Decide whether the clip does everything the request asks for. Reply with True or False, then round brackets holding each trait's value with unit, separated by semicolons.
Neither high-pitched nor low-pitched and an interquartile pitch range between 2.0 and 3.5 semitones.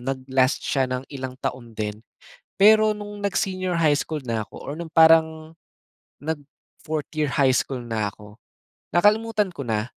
False (145 Hz; 5.4 semitones)